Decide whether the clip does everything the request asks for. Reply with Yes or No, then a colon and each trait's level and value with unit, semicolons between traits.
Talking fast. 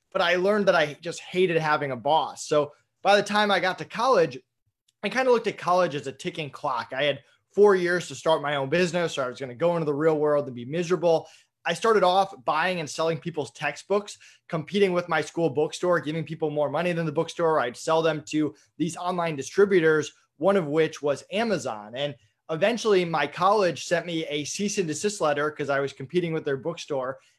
Yes: fast, 220 wpm